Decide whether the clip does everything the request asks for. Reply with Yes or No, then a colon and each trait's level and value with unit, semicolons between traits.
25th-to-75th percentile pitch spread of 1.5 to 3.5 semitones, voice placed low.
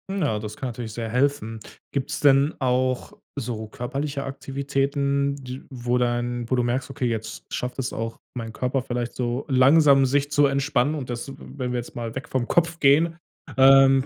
Yes: narrow, 2.4 semitones; low, 130 Hz